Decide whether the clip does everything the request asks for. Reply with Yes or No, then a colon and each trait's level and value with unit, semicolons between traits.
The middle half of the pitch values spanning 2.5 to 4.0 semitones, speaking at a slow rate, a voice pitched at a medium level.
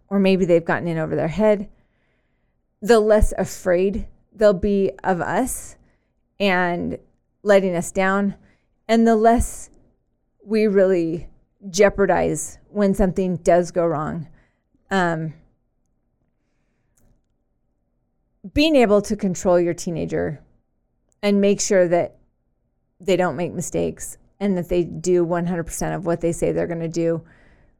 Yes: average, 3.1 semitones; slow, 125 wpm; medium, 180 Hz